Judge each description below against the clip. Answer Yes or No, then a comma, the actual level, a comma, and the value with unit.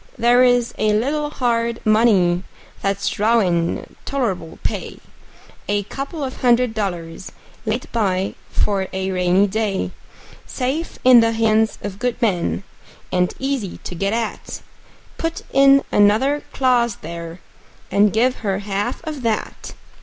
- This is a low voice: No, high, 220 Hz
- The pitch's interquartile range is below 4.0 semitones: No, average, 4.3 semitones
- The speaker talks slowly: Yes, slow, 130 wpm